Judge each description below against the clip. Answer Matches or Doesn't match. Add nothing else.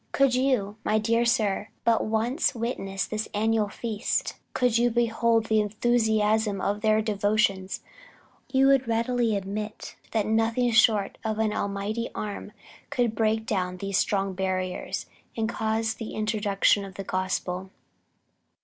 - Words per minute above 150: Doesn't match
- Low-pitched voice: Doesn't match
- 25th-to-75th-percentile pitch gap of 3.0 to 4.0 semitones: Doesn't match